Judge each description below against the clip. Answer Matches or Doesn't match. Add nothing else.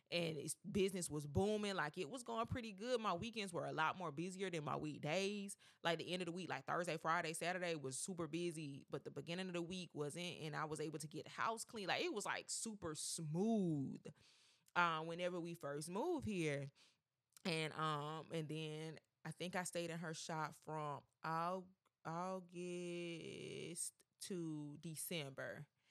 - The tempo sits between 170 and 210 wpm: Matches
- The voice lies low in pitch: Doesn't match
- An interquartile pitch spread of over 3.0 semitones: Doesn't match